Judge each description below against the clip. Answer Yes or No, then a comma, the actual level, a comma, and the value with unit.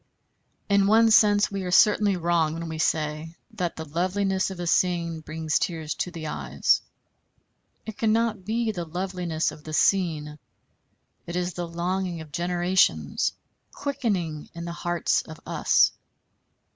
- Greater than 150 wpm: No, average, 145 wpm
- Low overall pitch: No, medium, 175 Hz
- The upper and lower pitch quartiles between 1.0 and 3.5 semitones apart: Yes, average, 3.2 semitones